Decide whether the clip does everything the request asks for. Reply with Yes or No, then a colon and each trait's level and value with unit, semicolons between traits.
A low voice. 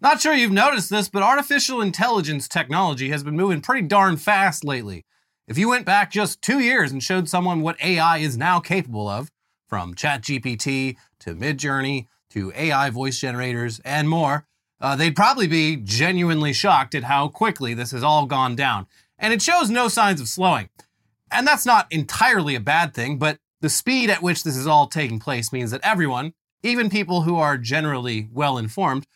No: medium, 155 Hz